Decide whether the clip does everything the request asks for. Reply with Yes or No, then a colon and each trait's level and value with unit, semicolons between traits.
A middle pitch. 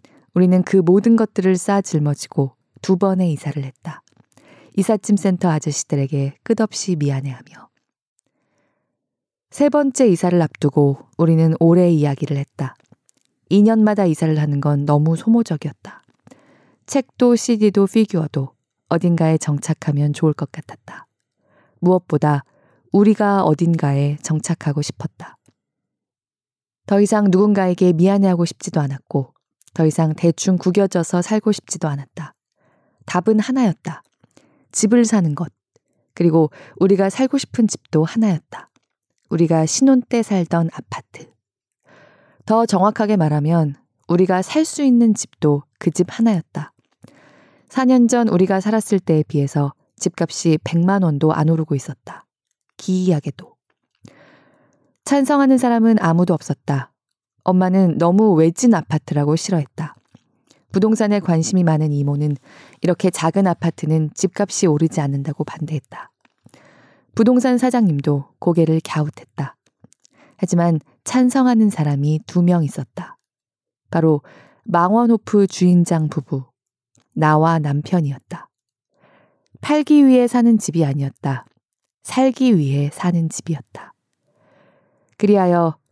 Yes: medium, 170 Hz